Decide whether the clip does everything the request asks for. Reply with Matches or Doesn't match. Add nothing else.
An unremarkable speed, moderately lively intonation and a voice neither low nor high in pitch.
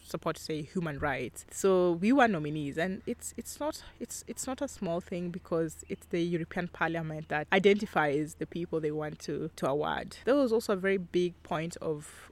Matches